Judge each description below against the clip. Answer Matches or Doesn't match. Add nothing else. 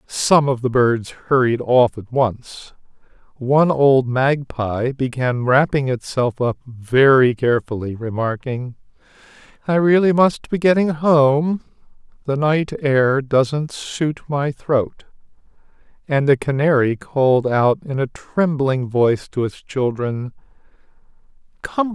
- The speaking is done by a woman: Doesn't match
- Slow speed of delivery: Matches